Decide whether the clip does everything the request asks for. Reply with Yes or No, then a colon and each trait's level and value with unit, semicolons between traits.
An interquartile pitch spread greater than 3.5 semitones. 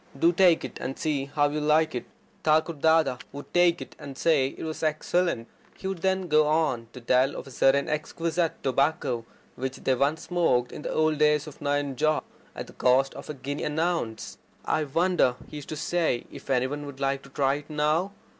No: average, 2.9 semitones